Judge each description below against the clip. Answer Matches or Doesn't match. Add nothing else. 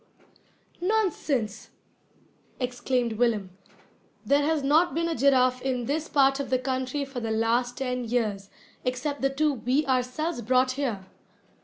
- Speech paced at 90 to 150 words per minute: Matches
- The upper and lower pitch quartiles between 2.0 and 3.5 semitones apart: Matches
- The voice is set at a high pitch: Matches